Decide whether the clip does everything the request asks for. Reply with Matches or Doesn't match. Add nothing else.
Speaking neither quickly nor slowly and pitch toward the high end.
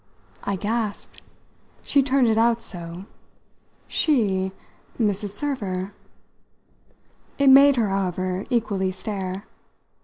Doesn't match